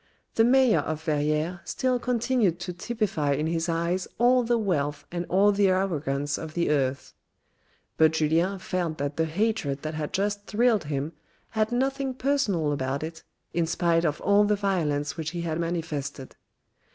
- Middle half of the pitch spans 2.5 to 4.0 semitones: No, average, 5.2 semitones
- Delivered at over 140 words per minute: Yes, average, 165 wpm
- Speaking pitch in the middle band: Yes, medium, 170 Hz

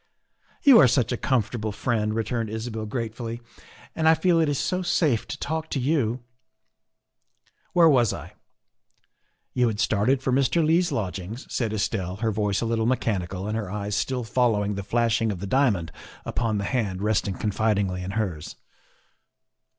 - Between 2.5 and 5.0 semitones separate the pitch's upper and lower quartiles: Yes, average, 3.9 semitones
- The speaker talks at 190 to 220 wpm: No, average, 175 wpm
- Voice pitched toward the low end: Yes, low, 115 Hz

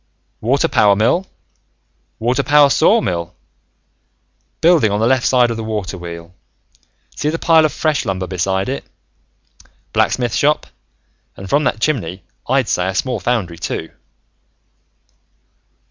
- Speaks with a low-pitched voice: Yes, low, 115 Hz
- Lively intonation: Yes, wide, 6.9 semitones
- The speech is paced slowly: Yes, slow, 130 wpm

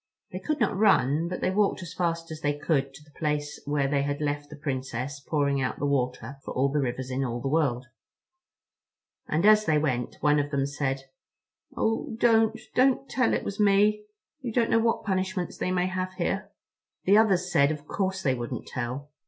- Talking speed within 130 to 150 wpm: No, average, 200 wpm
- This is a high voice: No, medium, 150 Hz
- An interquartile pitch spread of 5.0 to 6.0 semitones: Yes, wide, 5.6 semitones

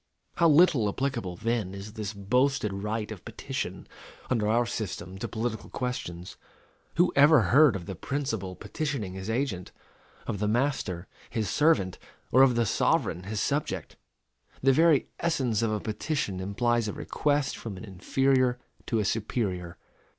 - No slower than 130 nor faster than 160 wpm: Yes, average, 150 wpm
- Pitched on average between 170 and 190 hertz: No, low, 115 Hz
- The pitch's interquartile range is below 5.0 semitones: No, average, 5.3 semitones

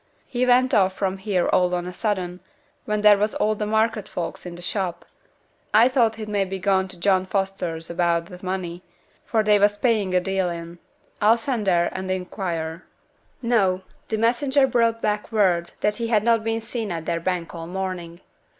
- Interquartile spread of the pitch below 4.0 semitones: Yes, average, 3.5 semitones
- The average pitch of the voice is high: Yes, high, 195 Hz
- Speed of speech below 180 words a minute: No, average, 190 wpm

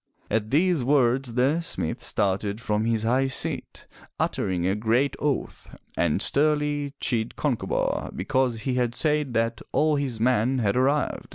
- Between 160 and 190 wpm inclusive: No, average, 150 wpm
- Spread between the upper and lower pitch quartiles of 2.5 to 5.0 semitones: Yes, average, 4.2 semitones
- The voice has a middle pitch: No, low, 125 Hz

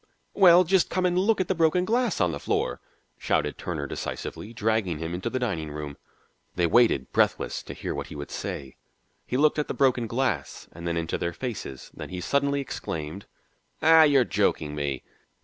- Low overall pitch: Yes, low, 110 Hz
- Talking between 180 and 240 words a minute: Yes, average, 190 wpm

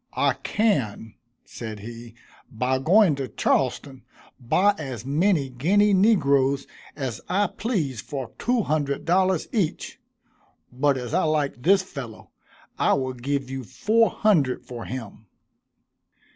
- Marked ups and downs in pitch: Yes, wide, 6.9 semitones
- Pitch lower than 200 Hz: Yes, medium, 140 Hz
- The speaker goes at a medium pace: No, slow, 130 wpm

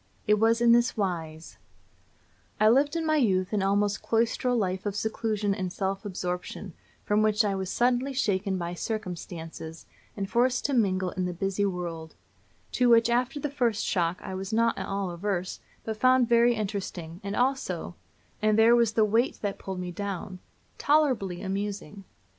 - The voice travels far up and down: No, average, 3.8 semitones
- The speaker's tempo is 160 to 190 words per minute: Yes, average, 170 wpm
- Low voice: No, high, 205 Hz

